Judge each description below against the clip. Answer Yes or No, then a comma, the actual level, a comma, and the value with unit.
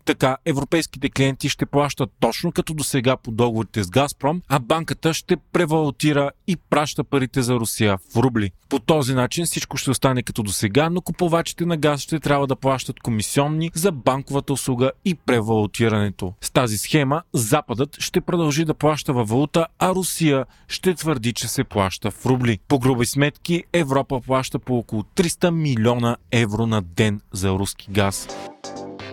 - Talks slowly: No, fast, 165 wpm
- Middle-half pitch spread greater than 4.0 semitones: Yes, average, 4.7 semitones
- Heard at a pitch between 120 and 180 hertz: Yes, low, 135 Hz